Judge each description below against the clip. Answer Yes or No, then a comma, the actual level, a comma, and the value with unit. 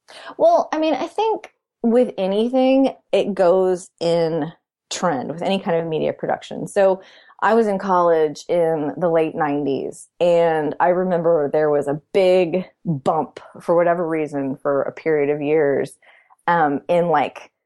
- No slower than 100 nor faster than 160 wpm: Yes, average, 155 wpm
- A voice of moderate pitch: Yes, medium, 170 Hz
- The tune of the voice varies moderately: Yes, average, 3.7 semitones